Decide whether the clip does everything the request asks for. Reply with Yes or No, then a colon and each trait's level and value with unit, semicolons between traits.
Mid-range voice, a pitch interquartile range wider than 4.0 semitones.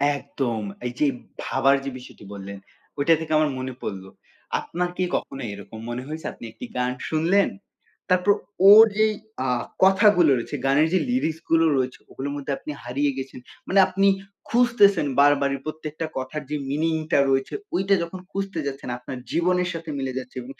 Yes: medium, 150 Hz; average, 5.3 semitones